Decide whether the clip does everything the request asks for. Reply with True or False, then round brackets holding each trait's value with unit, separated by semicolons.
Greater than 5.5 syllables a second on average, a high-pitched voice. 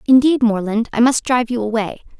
True (6.0 syllables/s; 235 Hz)